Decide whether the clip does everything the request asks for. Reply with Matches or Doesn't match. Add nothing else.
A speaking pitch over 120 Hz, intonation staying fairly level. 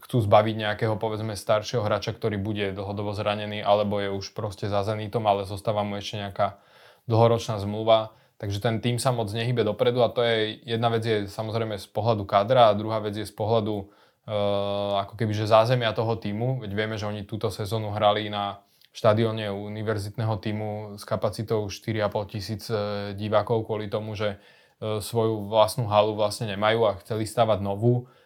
Doesn't match